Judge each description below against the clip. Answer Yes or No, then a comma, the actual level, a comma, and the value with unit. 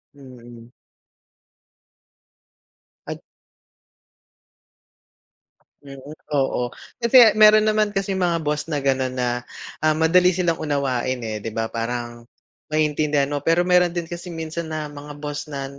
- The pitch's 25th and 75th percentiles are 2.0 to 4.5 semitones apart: No, average, 5.0 semitones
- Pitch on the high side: No, medium, 150 Hz